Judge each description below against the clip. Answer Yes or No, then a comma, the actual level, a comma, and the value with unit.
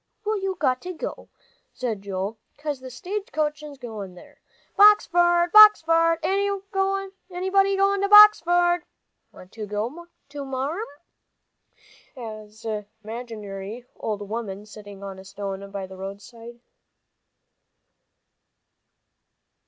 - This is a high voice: Yes, very high, 255 Hz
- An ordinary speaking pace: No, slow, 100 wpm